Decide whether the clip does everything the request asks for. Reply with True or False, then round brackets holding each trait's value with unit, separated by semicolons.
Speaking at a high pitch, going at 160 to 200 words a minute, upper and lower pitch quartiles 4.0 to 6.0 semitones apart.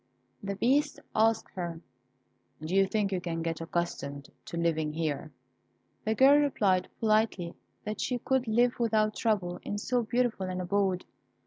False (200 Hz; 150 wpm; 4.7 semitones)